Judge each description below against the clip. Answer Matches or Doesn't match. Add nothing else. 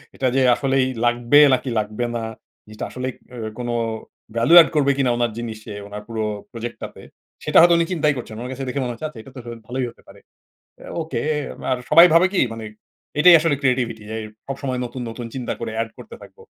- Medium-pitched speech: Doesn't match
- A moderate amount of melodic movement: Matches